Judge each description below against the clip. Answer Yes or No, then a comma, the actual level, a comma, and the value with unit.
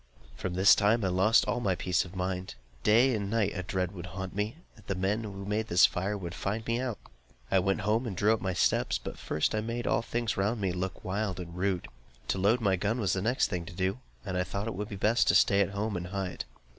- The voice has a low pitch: Yes, low, 100 Hz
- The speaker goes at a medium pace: No, fast, 260 wpm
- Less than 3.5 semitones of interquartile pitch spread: Yes, average, 2.8 semitones